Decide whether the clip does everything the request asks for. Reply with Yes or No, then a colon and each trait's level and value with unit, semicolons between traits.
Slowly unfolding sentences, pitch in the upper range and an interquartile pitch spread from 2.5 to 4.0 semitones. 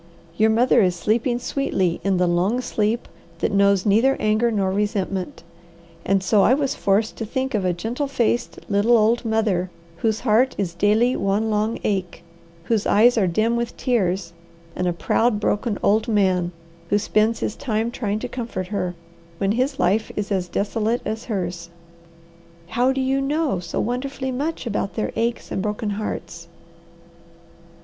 No: average, 165 wpm; high, 215 Hz; average, 3.4 semitones